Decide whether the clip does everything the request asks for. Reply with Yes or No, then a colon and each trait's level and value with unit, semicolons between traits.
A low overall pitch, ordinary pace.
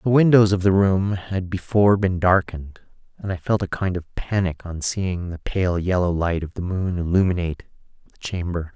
Yes: very low, 90 Hz; average, 190 wpm